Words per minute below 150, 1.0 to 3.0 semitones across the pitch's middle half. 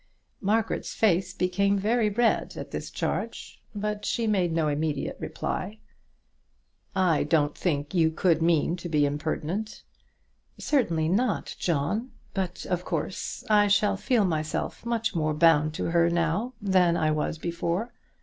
No: average, 140 wpm; average, 4.5 semitones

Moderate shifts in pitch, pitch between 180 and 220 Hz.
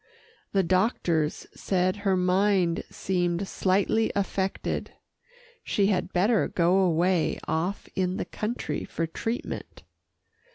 No: narrow, 2.1 semitones; medium, 185 Hz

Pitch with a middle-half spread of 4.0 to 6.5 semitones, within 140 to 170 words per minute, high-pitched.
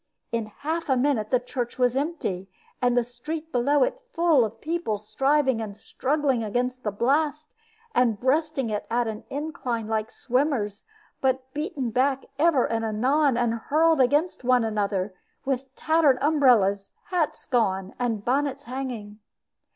Yes: average, 4.5 semitones; average, 150 wpm; very high, 255 Hz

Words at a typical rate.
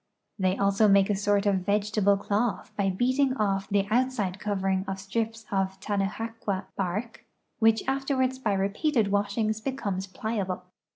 Yes: average, 150 wpm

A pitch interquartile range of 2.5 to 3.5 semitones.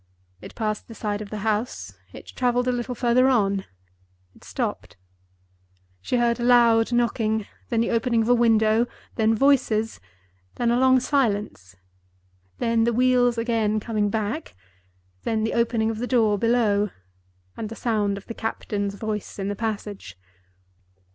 Yes: average, 2.8 semitones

